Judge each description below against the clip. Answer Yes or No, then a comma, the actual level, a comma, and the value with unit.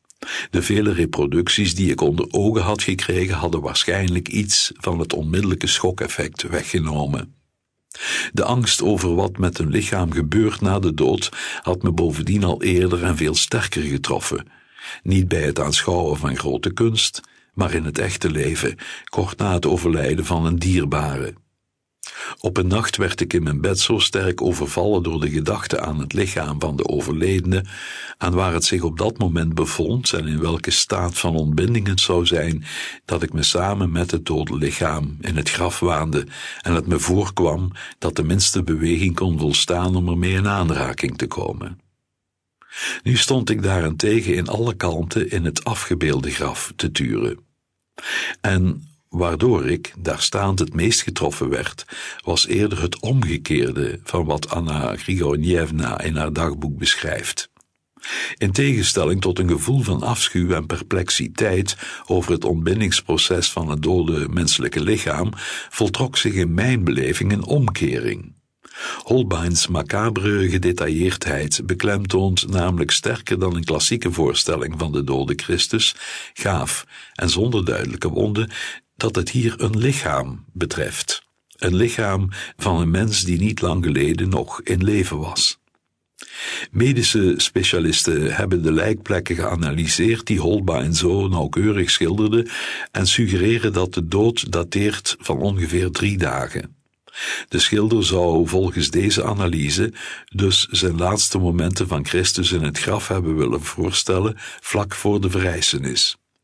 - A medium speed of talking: Yes, average, 145 wpm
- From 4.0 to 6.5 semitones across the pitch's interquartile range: No, average, 3.5 semitones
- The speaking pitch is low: Yes, very low, 90 Hz